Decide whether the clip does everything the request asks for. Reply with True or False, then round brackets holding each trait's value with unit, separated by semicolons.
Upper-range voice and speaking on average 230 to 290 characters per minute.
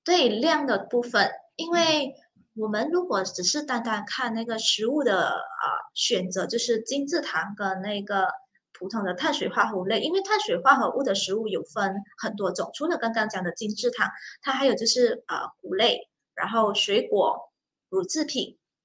True (230 Hz; 260 characters per minute)